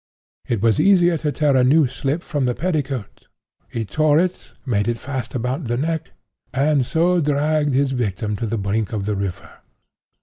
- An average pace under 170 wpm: No, average, 180 wpm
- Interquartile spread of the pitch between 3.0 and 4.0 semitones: No, average, 5.0 semitones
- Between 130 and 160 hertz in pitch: Yes, low, 135 Hz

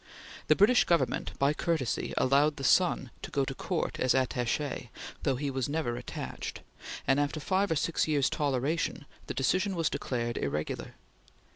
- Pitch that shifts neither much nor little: Yes, average, 3.9 semitones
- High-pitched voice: No, medium, 140 Hz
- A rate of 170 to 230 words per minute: No, average, 160 wpm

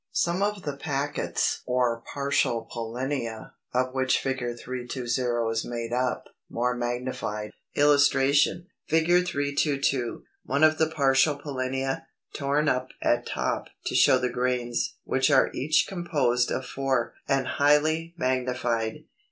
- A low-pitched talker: Yes, low, 130 Hz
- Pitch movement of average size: Yes, average, 3.0 semitones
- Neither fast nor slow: No, slow, 125 wpm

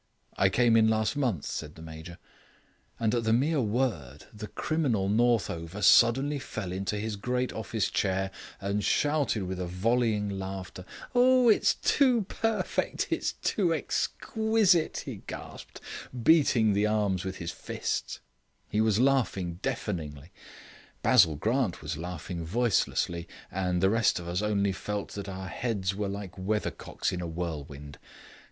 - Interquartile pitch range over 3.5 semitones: Yes, average, 5.0 semitones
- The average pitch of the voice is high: No, low, 105 Hz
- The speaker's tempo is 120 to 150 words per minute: Yes, average, 145 wpm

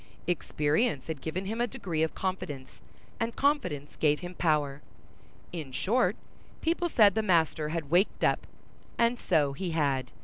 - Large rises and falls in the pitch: Yes, wide, 6.2 semitones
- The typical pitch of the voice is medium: Yes, medium, 165 Hz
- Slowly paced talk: No, average, 150 wpm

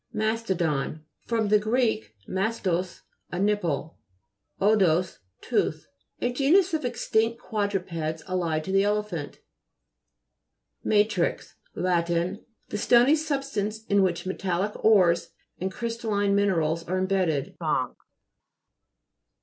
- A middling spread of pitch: Yes, average, 4.1 semitones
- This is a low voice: No, high, 200 Hz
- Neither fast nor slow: No, slow, 100 wpm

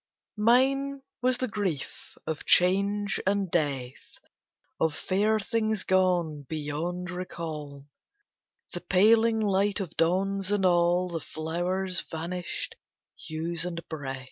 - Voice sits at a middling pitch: Yes, medium, 180 Hz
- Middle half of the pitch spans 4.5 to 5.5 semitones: No, average, 4.0 semitones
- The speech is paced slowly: Yes, slow, 115 wpm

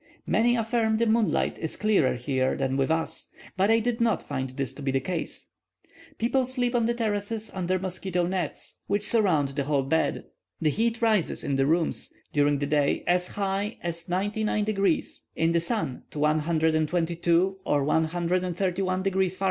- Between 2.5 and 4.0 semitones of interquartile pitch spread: No, wide, 5.4 semitones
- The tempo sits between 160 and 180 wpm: Yes, average, 170 wpm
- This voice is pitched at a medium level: Yes, medium, 180 Hz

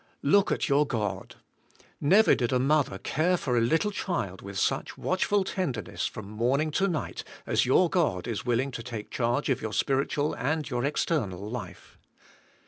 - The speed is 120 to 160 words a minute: No, average, 170 wpm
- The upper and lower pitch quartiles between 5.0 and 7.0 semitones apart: Yes, wide, 5.5 semitones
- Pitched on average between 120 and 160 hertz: Yes, low, 135 Hz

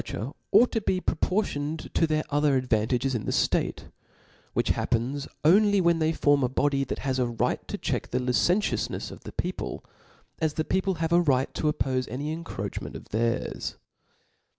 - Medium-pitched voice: Yes, medium, 145 Hz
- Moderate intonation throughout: Yes, average, 4.6 semitones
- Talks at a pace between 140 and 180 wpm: No, average, 190 wpm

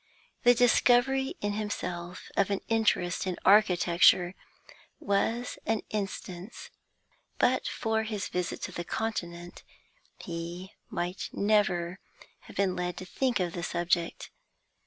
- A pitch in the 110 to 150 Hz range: No, high, 190 Hz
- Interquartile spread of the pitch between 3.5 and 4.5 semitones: Yes, average, 3.9 semitones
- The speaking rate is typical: No, slow, 120 wpm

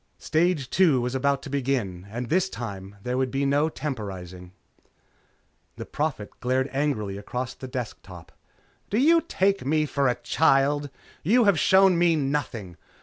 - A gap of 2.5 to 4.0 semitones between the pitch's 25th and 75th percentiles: No, average, 4.9 semitones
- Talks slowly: No, average, 155 wpm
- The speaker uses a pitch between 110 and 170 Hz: Yes, low, 135 Hz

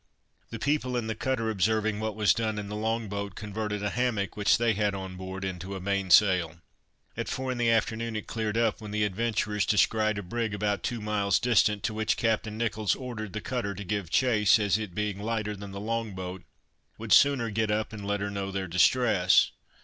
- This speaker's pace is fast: Yes, fast, 215 wpm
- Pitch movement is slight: Yes, narrow, 2.1 semitones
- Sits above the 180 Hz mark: No, low, 105 Hz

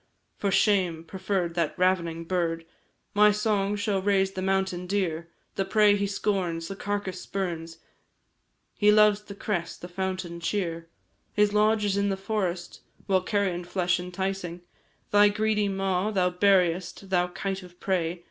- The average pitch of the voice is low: No, high, 190 Hz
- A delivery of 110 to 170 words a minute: Yes, average, 150 wpm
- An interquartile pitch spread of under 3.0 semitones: Yes, narrow, 2.4 semitones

